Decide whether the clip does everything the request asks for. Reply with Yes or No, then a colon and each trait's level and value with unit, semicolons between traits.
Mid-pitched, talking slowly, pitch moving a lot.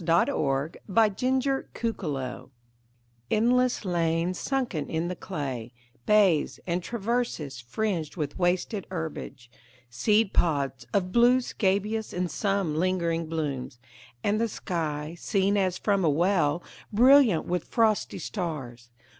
Yes: medium, 180 Hz; slow, 120 wpm; wide, 5.7 semitones